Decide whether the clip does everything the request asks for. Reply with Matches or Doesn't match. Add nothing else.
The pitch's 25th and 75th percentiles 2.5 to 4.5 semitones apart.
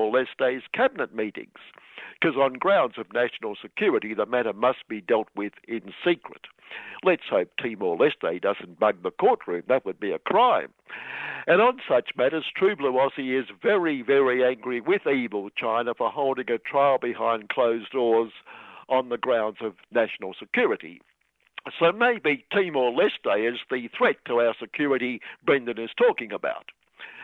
Matches